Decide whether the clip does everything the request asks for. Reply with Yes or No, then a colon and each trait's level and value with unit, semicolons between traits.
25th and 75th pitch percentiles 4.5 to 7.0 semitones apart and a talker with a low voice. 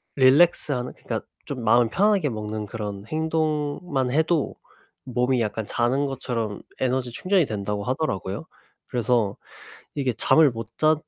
Yes: average, 5.0 semitones; low, 125 Hz